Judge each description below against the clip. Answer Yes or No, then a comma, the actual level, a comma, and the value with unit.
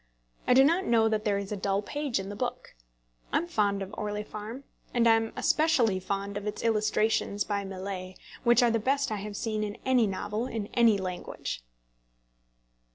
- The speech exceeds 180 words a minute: Yes, average, 190 wpm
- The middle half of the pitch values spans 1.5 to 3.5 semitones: Yes, average, 2.7 semitones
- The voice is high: Yes, high, 210 Hz